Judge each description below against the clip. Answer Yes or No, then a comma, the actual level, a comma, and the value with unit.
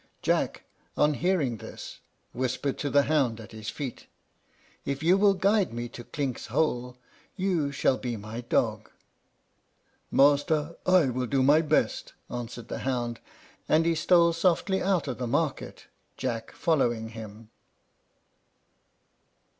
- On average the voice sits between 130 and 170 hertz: Yes, medium, 140 Hz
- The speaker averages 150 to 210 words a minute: No, slow, 135 wpm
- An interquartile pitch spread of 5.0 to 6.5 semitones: Yes, wide, 5.4 semitones